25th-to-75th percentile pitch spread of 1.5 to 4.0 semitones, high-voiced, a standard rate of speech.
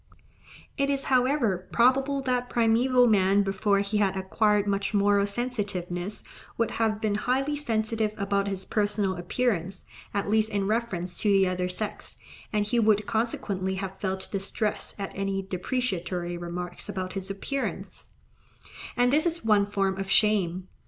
Yes: average, 3.3 semitones; high, 205 Hz; average, 150 wpm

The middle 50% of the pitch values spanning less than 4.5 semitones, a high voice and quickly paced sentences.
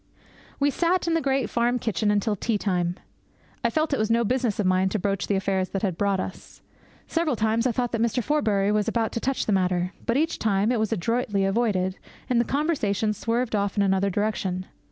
Yes: average, 3.7 semitones; high, 215 Hz; fast, 215 wpm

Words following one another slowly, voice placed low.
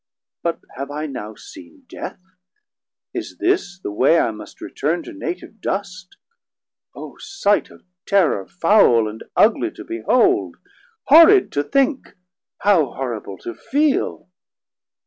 No: slow, 125 wpm; medium, 185 Hz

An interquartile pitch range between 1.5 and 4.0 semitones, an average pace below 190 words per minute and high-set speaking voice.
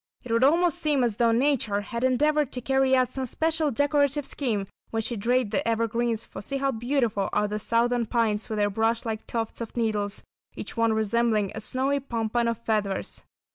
No: average, 3.4 semitones; average, 195 wpm; high, 235 Hz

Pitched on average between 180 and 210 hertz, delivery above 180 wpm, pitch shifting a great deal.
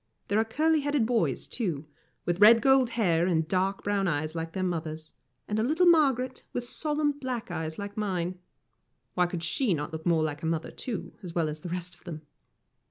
Yes: medium, 185 Hz; average, 200 wpm; wide, 6.7 semitones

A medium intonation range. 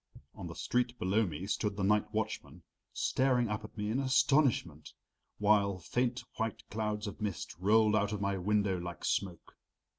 No: narrow, 2.3 semitones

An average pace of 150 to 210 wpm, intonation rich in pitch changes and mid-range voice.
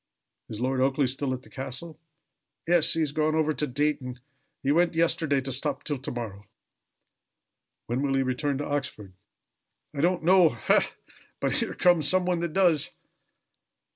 No: average, 165 wpm; average, 3.7 semitones; medium, 145 Hz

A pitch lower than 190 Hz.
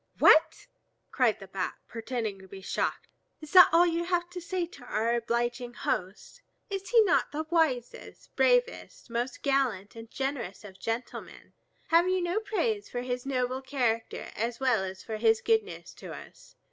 No: very high, 255 Hz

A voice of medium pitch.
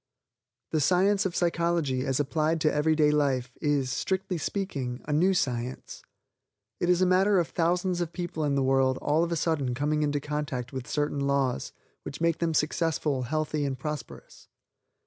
Yes: medium, 150 Hz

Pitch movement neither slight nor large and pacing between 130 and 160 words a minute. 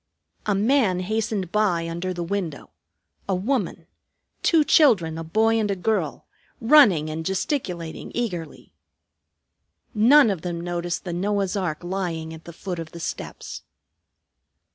Yes: average, 4.2 semitones; average, 140 wpm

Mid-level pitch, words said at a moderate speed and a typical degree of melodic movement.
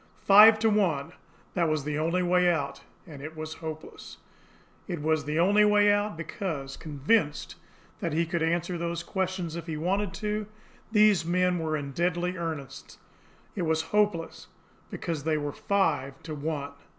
Yes: medium, 170 Hz; average, 160 wpm; average, 3.3 semitones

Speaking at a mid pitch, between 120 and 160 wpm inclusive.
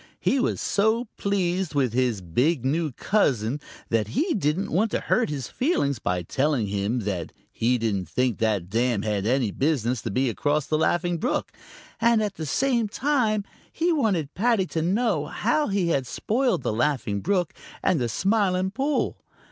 No: medium, 155 Hz; average, 170 wpm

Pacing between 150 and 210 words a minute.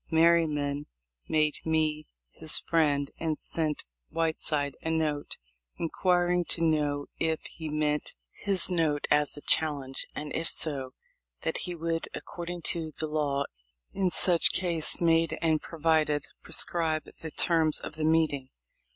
No: slow, 135 wpm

